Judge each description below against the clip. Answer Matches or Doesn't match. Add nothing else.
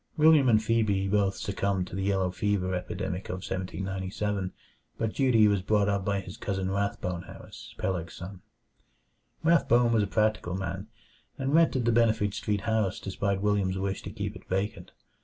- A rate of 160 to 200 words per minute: Matches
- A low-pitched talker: Matches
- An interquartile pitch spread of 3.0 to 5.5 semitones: Doesn't match